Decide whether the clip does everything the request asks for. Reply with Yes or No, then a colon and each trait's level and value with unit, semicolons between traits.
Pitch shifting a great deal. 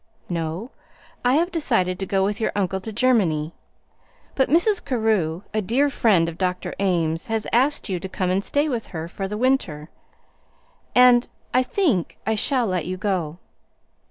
Yes: wide, 5.7 semitones